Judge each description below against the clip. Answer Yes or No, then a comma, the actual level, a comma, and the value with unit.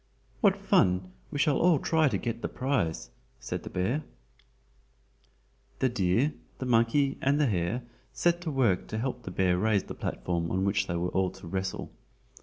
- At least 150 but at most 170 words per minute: No, average, 180 wpm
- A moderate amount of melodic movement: No, wide, 7.2 semitones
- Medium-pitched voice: No, low, 115 Hz